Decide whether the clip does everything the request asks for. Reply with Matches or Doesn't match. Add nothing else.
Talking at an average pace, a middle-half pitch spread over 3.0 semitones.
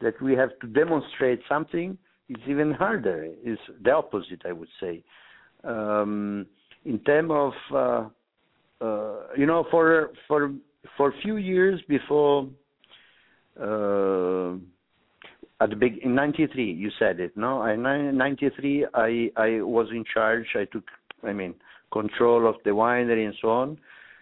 Matches